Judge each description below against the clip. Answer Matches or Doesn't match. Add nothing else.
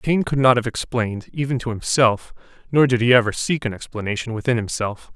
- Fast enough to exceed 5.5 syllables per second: Matches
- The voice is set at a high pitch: Doesn't match